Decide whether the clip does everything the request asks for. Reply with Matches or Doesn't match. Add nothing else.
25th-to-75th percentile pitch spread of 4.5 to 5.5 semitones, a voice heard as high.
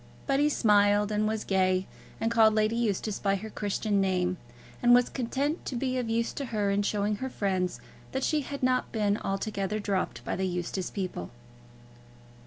Doesn't match